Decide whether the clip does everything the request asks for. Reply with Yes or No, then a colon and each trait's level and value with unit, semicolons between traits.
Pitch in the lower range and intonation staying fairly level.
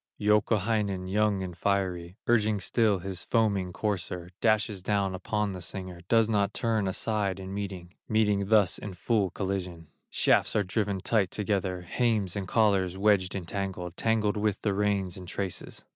Yes: low, 100 Hz; narrow, 2.3 semitones